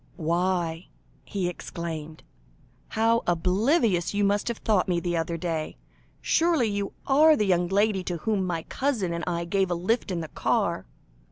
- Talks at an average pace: Yes, average, 165 wpm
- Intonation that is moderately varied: Yes, average, 3.9 semitones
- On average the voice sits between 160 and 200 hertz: Yes, medium, 185 Hz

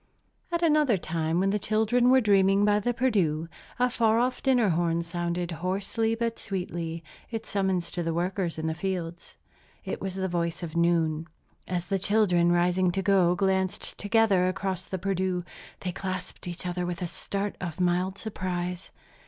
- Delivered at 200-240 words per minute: No, average, 170 wpm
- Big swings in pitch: No, average, 2.9 semitones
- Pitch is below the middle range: No, medium, 185 Hz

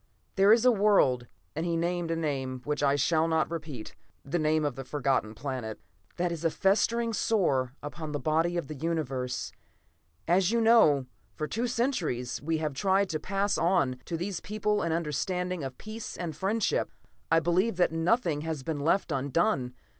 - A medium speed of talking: Yes, average, 180 wpm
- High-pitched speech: No, medium, 165 Hz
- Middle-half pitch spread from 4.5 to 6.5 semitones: Yes, average, 5.2 semitones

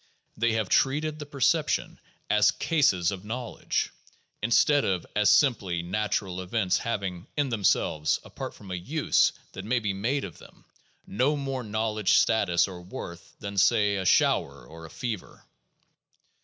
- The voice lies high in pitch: No, low, 105 Hz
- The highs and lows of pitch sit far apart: No, average, 4.8 semitones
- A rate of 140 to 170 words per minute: Yes, average, 150 wpm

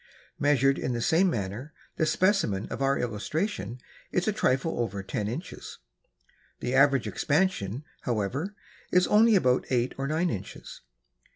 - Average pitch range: No, wide, 6.5 semitones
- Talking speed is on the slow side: No, average, 145 wpm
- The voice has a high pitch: No, low, 135 Hz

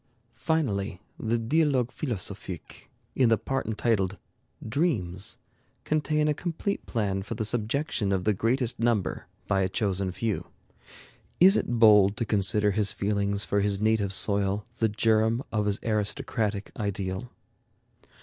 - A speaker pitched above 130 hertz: No, low, 110 Hz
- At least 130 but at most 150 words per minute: Yes, slow, 135 wpm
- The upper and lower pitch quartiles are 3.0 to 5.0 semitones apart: Yes, average, 3.4 semitones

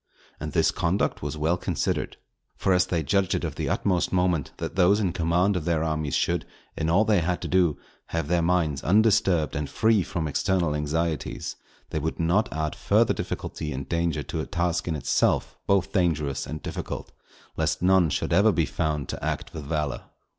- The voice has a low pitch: Yes, very low, 85 Hz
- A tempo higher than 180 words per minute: Yes, average, 190 wpm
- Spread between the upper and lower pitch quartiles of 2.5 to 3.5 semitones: Yes, average, 2.9 semitones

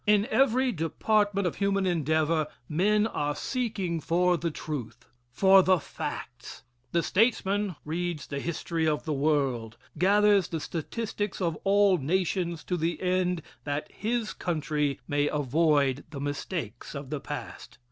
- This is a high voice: No, medium, 170 Hz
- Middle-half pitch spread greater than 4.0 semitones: Yes, average, 4.8 semitones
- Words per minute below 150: Yes, average, 140 wpm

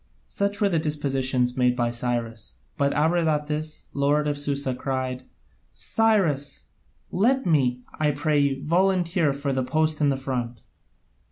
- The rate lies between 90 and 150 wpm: Yes, average, 140 wpm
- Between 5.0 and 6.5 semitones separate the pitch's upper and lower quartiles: No, average, 3.3 semitones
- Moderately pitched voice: Yes, medium, 145 Hz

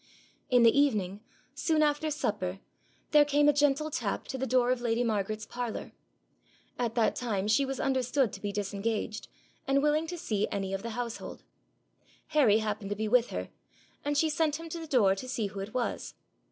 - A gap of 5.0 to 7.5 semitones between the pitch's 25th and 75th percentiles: Yes, wide, 5.4 semitones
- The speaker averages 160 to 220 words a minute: Yes, average, 195 wpm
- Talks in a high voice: Yes, high, 245 Hz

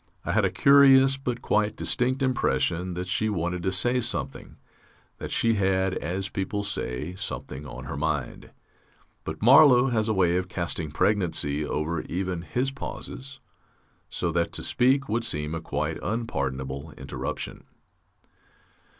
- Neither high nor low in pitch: No, very low, 95 Hz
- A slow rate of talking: No, average, 145 wpm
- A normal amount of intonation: No, wide, 7.1 semitones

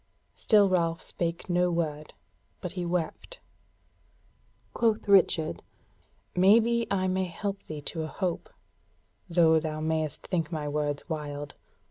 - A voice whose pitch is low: No, medium, 170 Hz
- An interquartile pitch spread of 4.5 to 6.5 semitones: No, average, 3.2 semitones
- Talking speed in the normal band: No, slow, 125 wpm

